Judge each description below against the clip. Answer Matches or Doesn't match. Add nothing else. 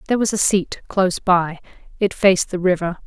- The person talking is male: Doesn't match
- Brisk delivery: Doesn't match